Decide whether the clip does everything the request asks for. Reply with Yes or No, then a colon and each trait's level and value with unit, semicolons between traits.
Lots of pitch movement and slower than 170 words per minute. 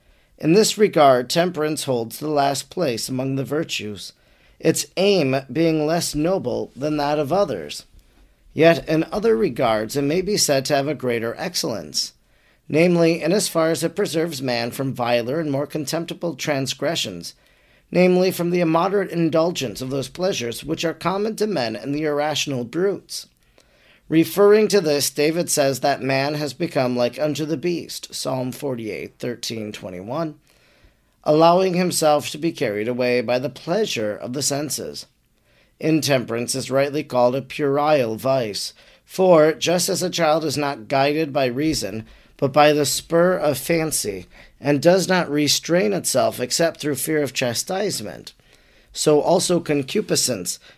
No: average, 4.0 semitones; average, 150 wpm